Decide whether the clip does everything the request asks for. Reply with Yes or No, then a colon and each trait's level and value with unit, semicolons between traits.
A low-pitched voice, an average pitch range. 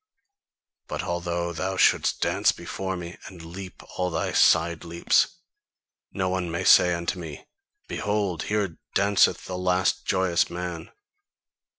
No: very low, 90 Hz; narrow, 1.6 semitones